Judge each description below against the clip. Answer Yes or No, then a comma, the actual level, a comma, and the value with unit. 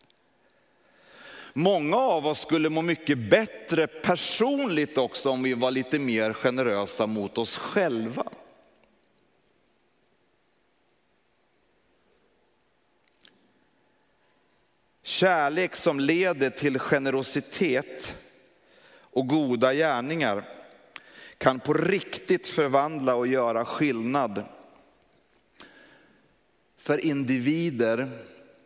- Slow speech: Yes, slow, 75 wpm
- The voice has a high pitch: No, medium, 140 Hz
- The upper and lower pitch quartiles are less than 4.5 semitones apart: Yes, average, 3.8 semitones